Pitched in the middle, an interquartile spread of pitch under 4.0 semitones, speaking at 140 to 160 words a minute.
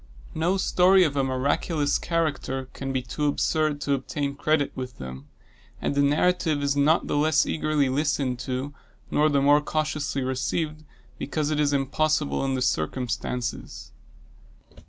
Yes: medium, 145 Hz; narrow, 2.5 semitones; average, 150 wpm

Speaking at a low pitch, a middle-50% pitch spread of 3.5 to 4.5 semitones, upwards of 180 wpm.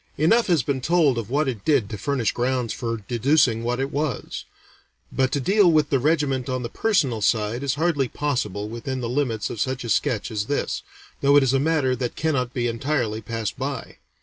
Yes: low, 130 Hz; average, 3.8 semitones; fast, 205 wpm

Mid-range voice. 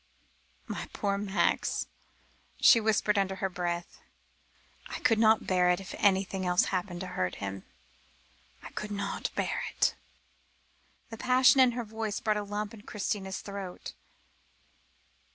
No: high, 200 Hz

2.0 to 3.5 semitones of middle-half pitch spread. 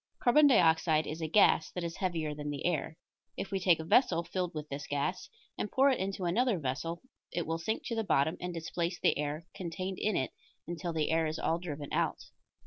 Yes: average, 3.1 semitones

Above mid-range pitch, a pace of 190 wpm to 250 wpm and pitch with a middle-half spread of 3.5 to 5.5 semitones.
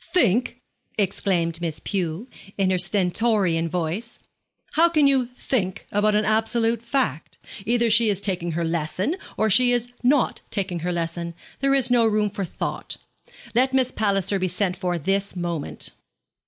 No: high, 200 Hz; average, 155 wpm; average, 5.1 semitones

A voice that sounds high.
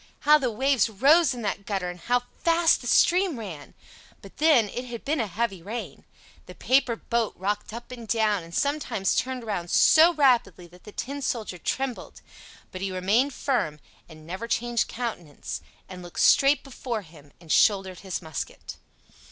Yes: high, 230 Hz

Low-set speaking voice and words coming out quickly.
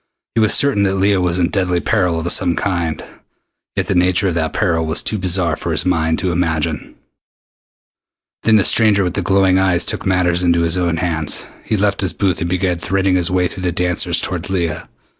Yes: very low, 90 Hz; fast, 210 wpm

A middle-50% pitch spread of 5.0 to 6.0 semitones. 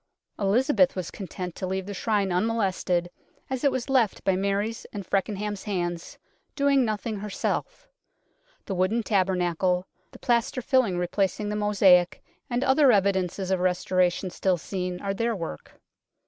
No: average, 3.5 semitones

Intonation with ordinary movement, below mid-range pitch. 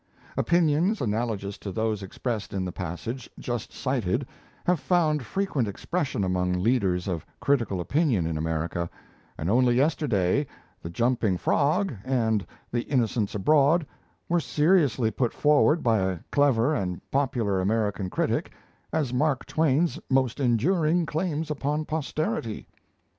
No: wide, 7.1 semitones; low, 125 Hz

